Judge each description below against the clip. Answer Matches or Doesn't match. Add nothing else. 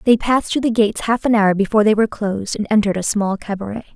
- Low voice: Doesn't match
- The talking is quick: Matches